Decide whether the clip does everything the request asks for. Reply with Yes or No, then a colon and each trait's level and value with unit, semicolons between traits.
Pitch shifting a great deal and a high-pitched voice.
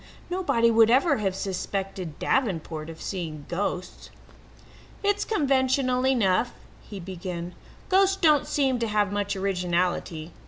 Yes: wide, 6.4 semitones; high, 205 Hz